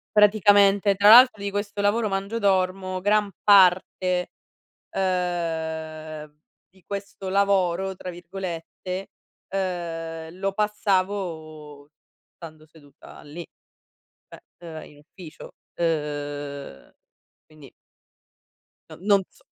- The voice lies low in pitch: No, medium, 185 Hz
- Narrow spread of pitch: No, average, 3.8 semitones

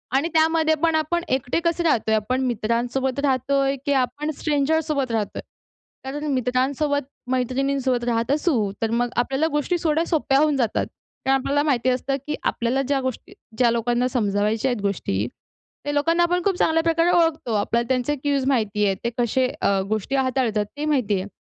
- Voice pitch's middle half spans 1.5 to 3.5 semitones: No, average, 3.9 semitones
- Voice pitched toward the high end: Yes, very high, 265 Hz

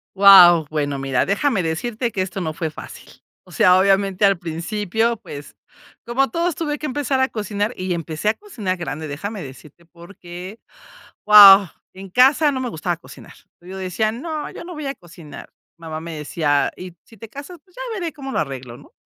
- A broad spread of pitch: Yes, wide, 6.4 semitones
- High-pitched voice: Yes, high, 195 Hz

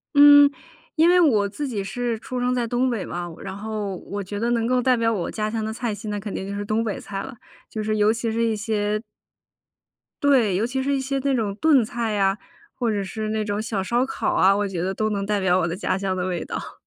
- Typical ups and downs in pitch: Yes, average, 3.3 semitones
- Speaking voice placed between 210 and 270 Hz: Yes, high, 215 Hz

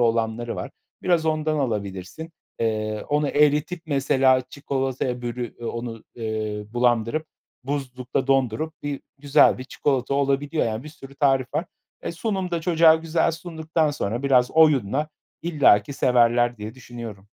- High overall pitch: No, low, 135 Hz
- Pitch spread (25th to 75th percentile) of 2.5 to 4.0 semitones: No, average, 4.5 semitones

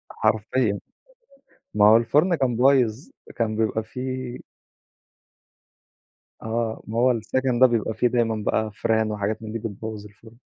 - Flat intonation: Yes, narrow, 2.3 semitones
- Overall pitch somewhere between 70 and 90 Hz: No, low, 115 Hz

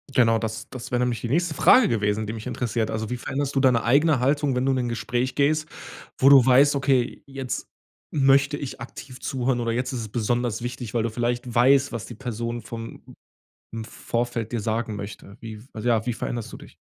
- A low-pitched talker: Yes, low, 120 Hz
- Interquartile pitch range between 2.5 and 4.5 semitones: Yes, average, 2.8 semitones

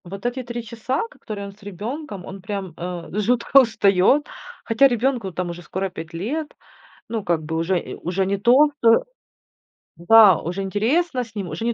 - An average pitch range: Yes, average, 4.9 semitones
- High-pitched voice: Yes, high, 205 Hz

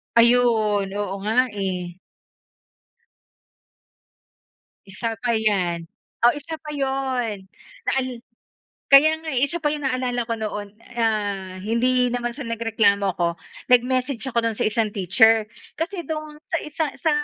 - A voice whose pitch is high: Yes, high, 235 Hz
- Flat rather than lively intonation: No, average, 4.2 semitones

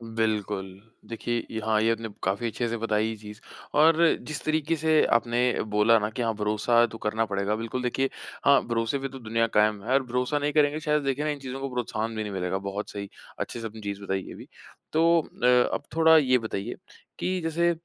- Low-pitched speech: Yes, low, 115 Hz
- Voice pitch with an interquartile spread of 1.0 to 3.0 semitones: No, average, 4.9 semitones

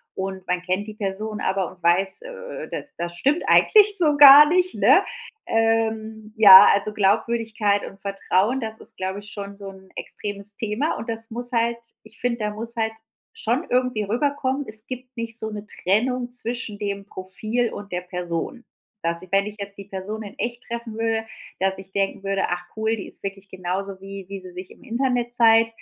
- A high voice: Yes, high, 215 Hz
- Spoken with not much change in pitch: No, average, 3.3 semitones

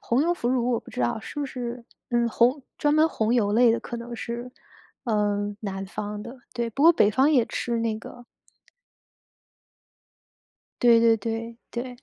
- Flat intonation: Yes, narrow, 2.1 semitones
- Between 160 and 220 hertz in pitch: No, high, 235 Hz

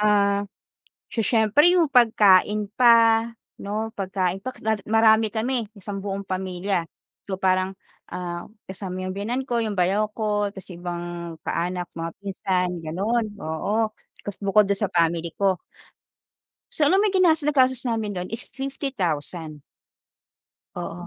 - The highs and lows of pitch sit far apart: No, average, 3.5 semitones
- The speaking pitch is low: No, high, 200 Hz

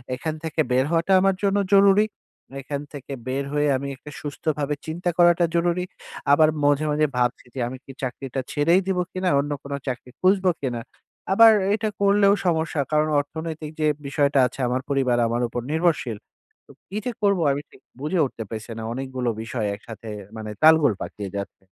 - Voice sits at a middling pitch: Yes, medium, 150 Hz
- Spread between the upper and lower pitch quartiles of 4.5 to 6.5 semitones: Yes, average, 5.0 semitones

